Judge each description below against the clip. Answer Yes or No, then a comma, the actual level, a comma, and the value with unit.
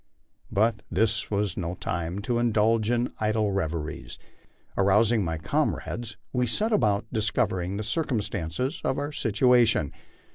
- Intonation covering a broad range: No, average, 3.6 semitones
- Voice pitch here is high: No, low, 110 Hz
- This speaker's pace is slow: Yes, slow, 130 wpm